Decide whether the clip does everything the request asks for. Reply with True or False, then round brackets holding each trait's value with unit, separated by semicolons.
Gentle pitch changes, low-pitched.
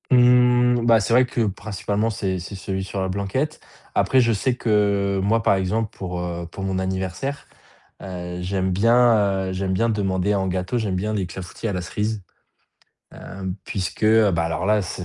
False (3.2 semitones; 100 Hz)